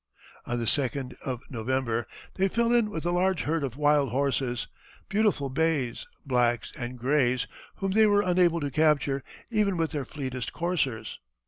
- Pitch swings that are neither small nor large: No, wide, 5.7 semitones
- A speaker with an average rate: Yes, average, 160 wpm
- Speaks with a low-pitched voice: No, medium, 145 Hz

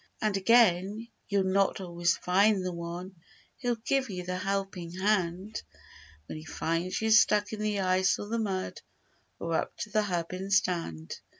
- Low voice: No, high, 190 Hz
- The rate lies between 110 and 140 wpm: No, average, 170 wpm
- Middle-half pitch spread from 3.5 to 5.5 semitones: No, average, 2.8 semitones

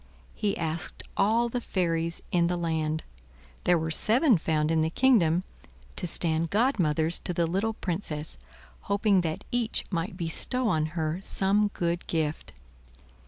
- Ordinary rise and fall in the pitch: Yes, average, 4.1 semitones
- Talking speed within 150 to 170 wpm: No, slow, 135 wpm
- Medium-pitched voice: Yes, medium, 170 Hz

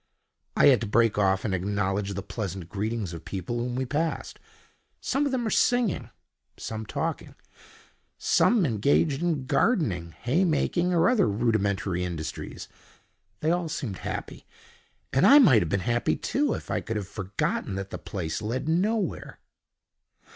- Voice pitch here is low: Yes, low, 115 Hz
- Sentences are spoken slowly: No, average, 155 wpm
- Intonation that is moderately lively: No, wide, 8.9 semitones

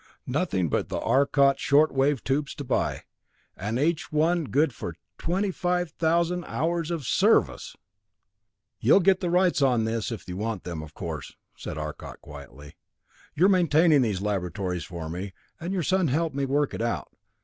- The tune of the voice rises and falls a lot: Yes, wide, 8.9 semitones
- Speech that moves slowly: No, average, 165 wpm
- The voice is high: No, medium, 140 Hz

